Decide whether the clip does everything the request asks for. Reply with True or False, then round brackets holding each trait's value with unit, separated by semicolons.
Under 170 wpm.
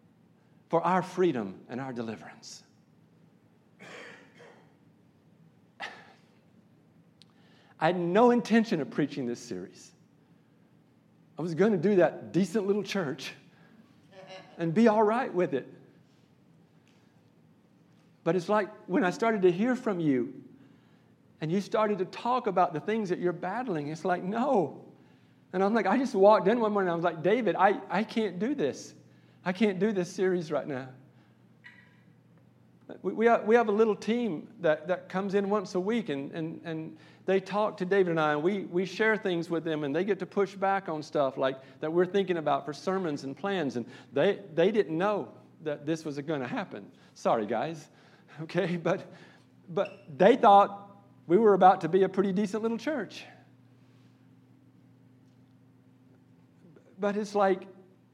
True (160 wpm)